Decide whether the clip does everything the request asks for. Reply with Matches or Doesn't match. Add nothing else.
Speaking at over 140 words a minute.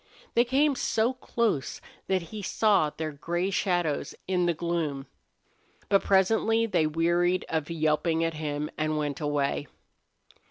Doesn't match